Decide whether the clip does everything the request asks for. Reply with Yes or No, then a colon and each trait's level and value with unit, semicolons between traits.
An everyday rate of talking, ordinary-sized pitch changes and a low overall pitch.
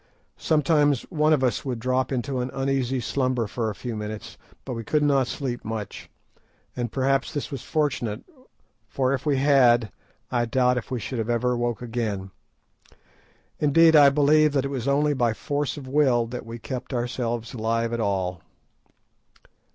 Yes: average, 170 wpm; average, 3.0 semitones; low, 125 Hz